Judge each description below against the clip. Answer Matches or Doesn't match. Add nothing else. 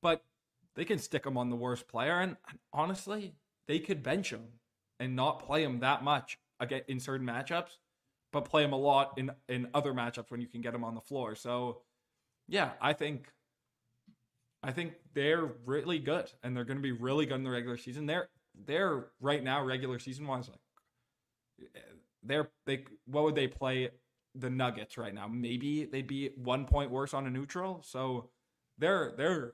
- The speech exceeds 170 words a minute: Matches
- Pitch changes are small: Doesn't match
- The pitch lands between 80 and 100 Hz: Doesn't match